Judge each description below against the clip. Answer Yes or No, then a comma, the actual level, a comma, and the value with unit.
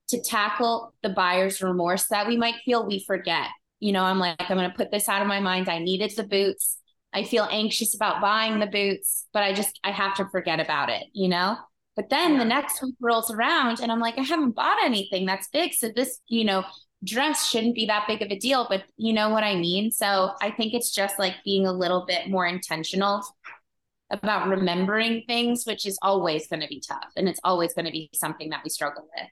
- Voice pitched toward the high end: Yes, high, 200 Hz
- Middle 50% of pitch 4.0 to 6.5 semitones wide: No, average, 3.6 semitones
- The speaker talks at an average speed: No, fast, 230 wpm